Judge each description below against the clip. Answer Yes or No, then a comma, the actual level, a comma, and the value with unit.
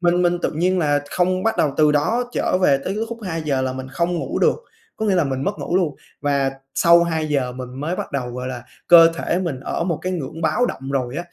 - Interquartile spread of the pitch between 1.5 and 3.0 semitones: No, average, 4.7 semitones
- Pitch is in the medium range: Yes, medium, 160 Hz